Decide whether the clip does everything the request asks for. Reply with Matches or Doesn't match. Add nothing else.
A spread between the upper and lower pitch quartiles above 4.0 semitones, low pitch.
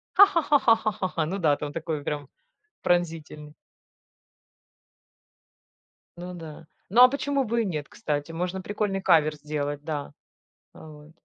Doesn't match